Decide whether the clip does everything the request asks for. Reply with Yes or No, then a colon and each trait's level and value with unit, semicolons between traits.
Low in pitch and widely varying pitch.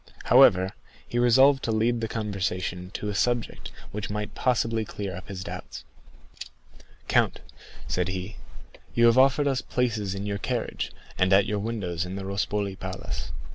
No: low, 105 Hz; average, 3.6 semitones